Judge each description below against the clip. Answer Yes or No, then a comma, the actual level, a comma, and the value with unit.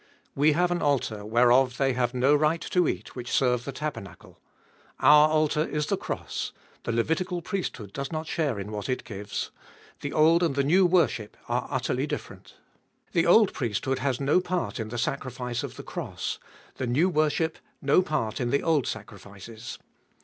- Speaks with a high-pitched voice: No, medium, 140 Hz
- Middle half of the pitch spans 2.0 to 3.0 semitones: No, average, 4.7 semitones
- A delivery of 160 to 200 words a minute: Yes, average, 180 wpm